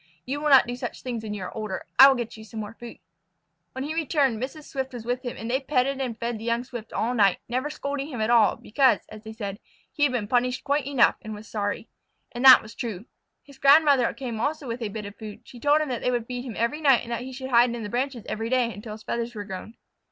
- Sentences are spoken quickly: Yes, fast, 270 wpm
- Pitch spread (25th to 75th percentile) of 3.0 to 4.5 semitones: Yes, average, 3.3 semitones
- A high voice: Yes, high, 240 Hz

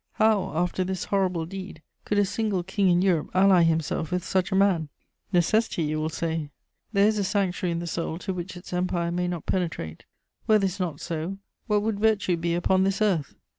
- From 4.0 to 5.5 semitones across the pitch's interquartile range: No, average, 2.7 semitones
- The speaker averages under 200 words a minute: No, fast, 205 wpm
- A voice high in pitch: No, medium, 180 Hz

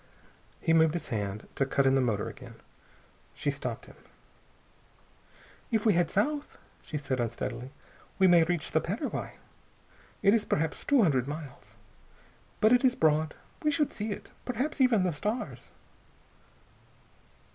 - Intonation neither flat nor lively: No, wide, 8.2 semitones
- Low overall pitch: No, medium, 165 Hz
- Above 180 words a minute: No, average, 145 wpm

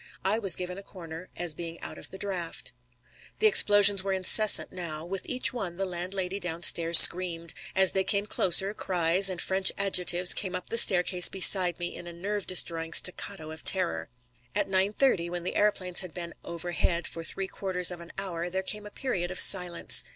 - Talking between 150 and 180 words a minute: No, average, 195 wpm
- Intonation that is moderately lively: No, narrow, 2.2 semitones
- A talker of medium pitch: Yes, medium, 180 Hz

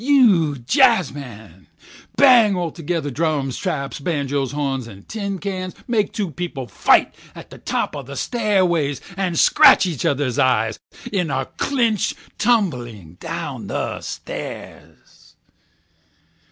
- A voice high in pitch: No, medium, 160 Hz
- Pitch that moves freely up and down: Yes, wide, 6.7 semitones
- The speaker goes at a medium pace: No, slow, 115 wpm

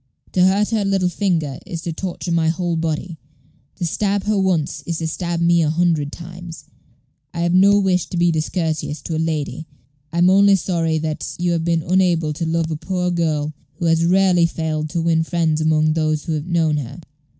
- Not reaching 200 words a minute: No, fast, 205 wpm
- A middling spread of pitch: No, narrow, 2.1 semitones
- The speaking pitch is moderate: Yes, medium, 170 Hz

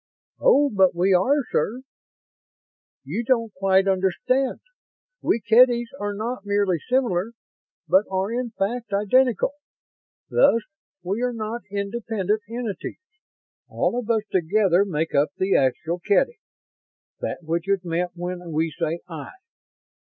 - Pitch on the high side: Yes, high, 200 Hz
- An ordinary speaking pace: No, slow, 130 wpm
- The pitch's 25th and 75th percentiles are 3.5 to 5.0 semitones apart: Yes, average, 4.7 semitones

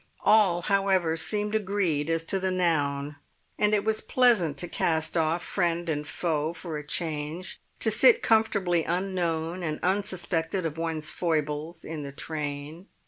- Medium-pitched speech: Yes, medium, 170 Hz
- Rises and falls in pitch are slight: No, average, 3.3 semitones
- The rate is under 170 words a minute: Yes, average, 150 wpm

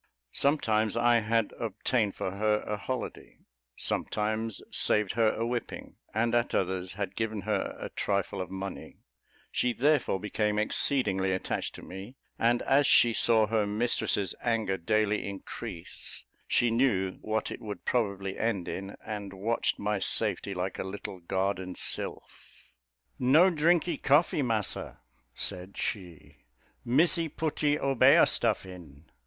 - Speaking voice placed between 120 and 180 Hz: No, low, 105 Hz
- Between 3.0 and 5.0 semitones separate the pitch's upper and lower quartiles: Yes, average, 3.6 semitones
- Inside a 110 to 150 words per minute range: Yes, slow, 135 wpm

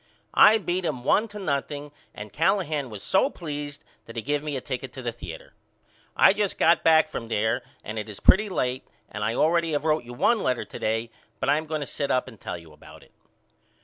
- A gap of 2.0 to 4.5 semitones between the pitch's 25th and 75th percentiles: No, wide, 5.5 semitones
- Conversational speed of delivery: No, fast, 230 wpm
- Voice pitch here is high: No, medium, 145 Hz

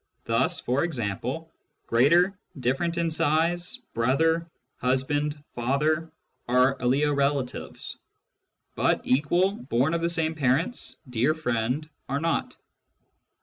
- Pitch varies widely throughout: No, average, 4.3 semitones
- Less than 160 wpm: Yes, average, 145 wpm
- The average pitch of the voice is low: No, medium, 145 Hz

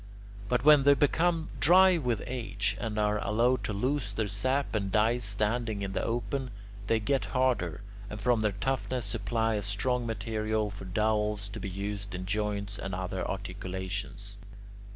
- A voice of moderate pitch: No, low, 110 Hz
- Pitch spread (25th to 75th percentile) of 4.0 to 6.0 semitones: No, average, 3.5 semitones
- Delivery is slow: No, average, 165 wpm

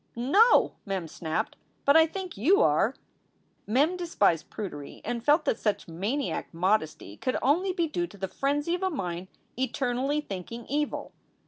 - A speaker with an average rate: Yes, average, 155 wpm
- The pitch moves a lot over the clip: Yes, wide, 8.6 semitones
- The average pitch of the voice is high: Yes, very high, 255 Hz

